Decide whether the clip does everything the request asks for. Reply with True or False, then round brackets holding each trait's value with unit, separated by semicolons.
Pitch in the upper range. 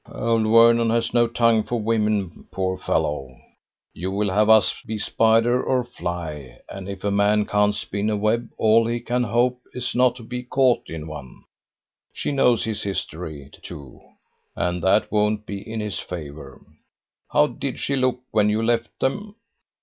False (110 Hz)